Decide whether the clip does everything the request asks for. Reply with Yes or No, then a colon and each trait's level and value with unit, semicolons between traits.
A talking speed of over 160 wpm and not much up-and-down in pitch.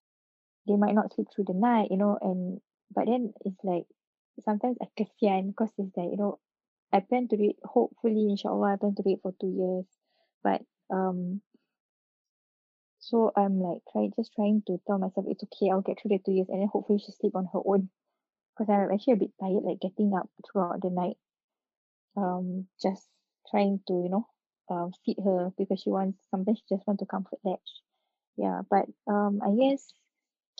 Yes: average, 200 wpm; narrow, 2.1 semitones